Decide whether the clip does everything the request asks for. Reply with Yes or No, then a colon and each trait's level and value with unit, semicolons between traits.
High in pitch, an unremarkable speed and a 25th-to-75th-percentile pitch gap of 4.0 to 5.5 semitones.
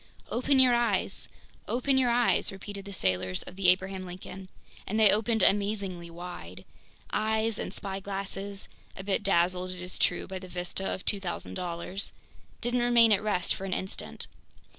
No: high, 195 Hz; average, 160 wpm; average, 3.0 semitones